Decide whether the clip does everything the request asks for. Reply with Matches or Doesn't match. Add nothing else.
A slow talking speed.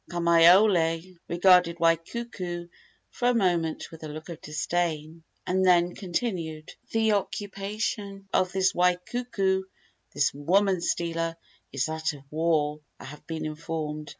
Matches